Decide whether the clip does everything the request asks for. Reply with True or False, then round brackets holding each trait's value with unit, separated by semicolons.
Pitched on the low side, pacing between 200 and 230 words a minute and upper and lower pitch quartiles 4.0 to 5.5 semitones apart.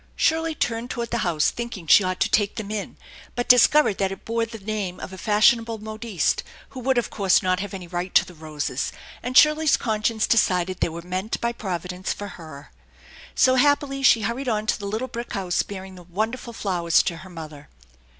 False (210 Hz; 205 wpm; 4.5 semitones)